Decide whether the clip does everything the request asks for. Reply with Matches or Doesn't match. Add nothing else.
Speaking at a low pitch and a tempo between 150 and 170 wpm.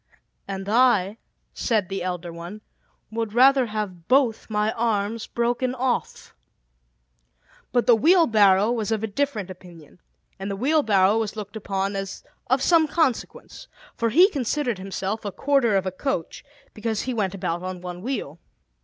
Doesn't match